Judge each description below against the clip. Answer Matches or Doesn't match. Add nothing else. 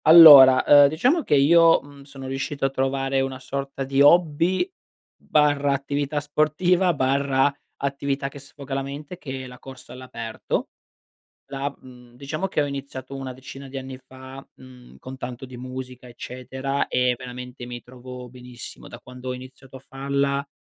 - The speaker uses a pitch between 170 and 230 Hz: Doesn't match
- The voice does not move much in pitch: Matches